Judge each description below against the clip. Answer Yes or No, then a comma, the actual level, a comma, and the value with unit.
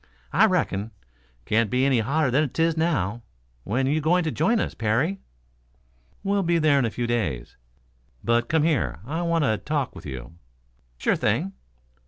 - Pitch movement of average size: No, wide, 6.2 semitones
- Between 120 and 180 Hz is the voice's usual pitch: Yes, medium, 140 Hz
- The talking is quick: No, average, 170 wpm